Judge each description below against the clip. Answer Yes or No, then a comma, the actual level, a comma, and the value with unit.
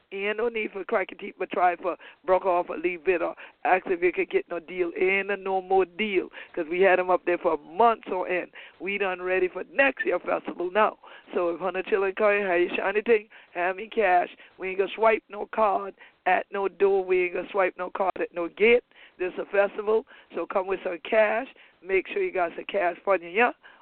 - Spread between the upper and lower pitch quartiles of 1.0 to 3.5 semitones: No, average, 4.3 semitones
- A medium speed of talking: No, fast, 245 wpm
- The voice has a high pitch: Yes, high, 195 Hz